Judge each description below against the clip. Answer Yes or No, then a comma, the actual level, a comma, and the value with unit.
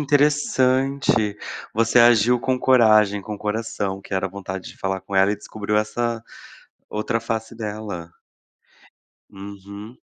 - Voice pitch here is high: No, low, 110 Hz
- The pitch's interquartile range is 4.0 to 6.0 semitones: No, average, 3.1 semitones